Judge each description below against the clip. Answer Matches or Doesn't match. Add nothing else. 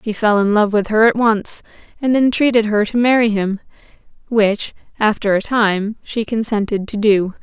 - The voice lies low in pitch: Doesn't match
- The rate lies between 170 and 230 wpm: Matches